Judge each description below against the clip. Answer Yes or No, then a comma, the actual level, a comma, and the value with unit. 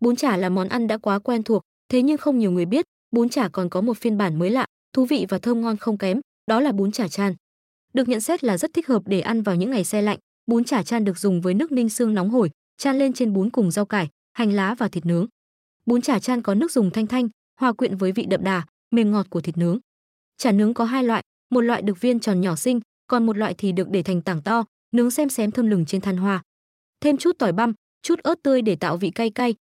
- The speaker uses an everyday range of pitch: Yes, average, 4.2 semitones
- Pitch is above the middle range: Yes, high, 225 Hz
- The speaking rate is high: Yes, fast, 270 wpm